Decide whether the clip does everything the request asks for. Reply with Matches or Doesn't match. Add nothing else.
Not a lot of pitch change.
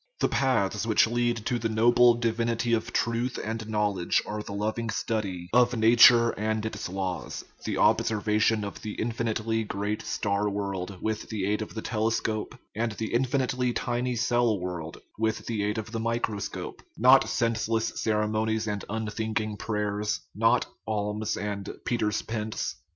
Matches